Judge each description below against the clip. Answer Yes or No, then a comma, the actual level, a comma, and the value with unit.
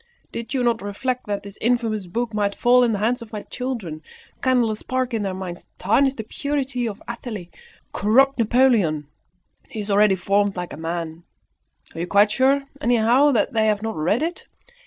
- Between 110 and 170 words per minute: No, average, 190 wpm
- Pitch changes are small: No, average, 3.8 semitones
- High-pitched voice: Yes, high, 220 Hz